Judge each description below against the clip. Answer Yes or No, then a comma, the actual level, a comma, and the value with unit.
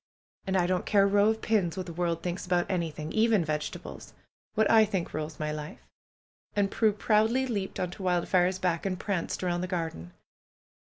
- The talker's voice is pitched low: No, medium, 185 Hz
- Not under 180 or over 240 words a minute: Yes, average, 190 wpm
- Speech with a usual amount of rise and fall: Yes, average, 3.3 semitones